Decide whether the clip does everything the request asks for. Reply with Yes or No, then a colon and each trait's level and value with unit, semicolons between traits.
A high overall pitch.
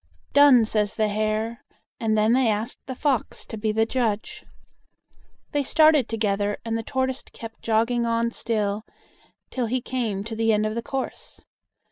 Yes: high, 225 Hz